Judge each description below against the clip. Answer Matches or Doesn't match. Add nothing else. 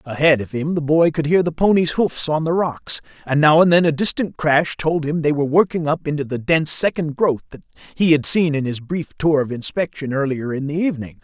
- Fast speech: Matches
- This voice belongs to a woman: Doesn't match